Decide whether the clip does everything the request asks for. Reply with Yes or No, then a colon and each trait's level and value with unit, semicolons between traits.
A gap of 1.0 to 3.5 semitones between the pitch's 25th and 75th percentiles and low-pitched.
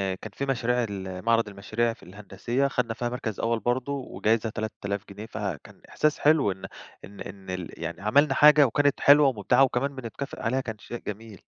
No: average, 4.6 semitones; low, 115 Hz